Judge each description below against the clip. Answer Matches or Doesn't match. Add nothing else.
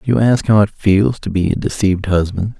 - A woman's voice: Doesn't match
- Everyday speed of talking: Doesn't match